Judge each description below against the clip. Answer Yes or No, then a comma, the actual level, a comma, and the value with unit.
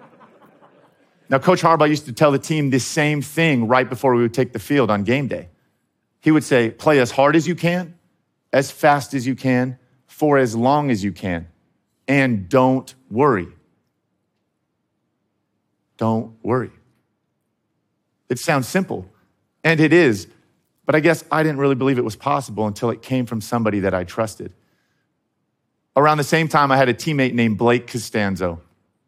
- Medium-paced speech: No, fast, 165 wpm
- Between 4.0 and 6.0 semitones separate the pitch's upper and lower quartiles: Yes, average, 4.5 semitones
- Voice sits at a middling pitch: No, low, 130 Hz